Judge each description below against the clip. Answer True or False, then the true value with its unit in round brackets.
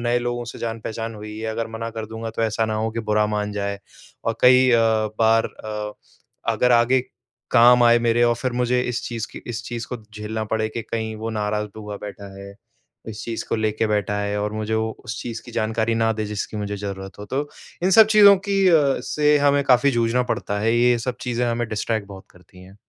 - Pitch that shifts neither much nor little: False (2.0 semitones)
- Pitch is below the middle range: True (110 Hz)